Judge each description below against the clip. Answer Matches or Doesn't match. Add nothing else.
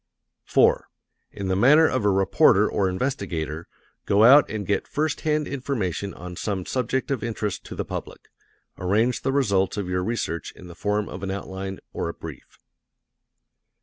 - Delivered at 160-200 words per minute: Matches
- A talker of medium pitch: Doesn't match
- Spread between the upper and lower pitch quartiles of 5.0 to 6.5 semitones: Matches